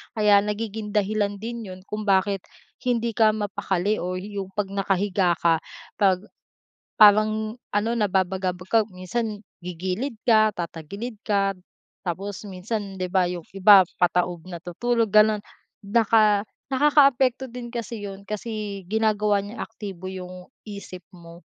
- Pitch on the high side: Yes, high, 205 Hz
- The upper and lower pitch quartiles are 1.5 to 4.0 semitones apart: Yes, average, 2.8 semitones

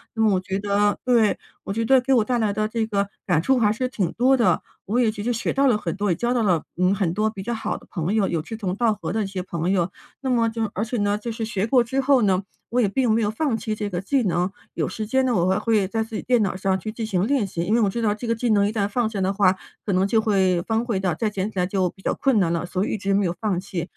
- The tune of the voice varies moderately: Yes, average, 3.2 semitones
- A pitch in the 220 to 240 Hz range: No, high, 210 Hz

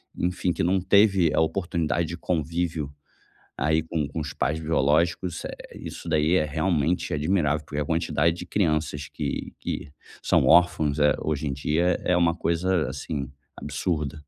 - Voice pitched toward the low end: Yes, very low, 80 Hz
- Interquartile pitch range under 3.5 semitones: Yes, average, 2.7 semitones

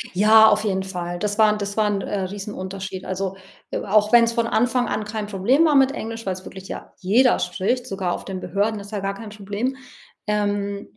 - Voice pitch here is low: No, high, 205 Hz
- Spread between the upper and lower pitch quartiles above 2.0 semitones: Yes, narrow, 2.4 semitones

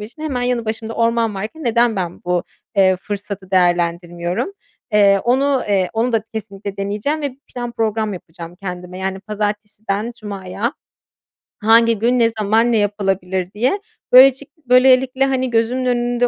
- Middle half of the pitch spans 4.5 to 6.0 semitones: No, average, 3.9 semitones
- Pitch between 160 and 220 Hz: Yes, high, 215 Hz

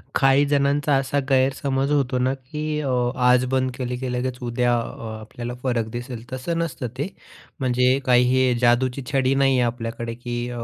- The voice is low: Yes, low, 130 Hz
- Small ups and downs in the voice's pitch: Yes, narrow, 1.8 semitones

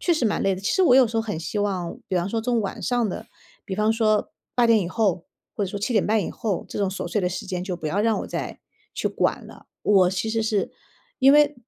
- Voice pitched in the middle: No, high, 210 Hz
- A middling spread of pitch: Yes, average, 3.3 semitones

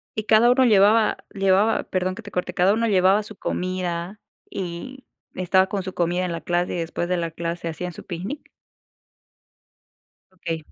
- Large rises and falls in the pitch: No, average, 2.9 semitones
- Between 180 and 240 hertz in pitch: Yes, medium, 185 Hz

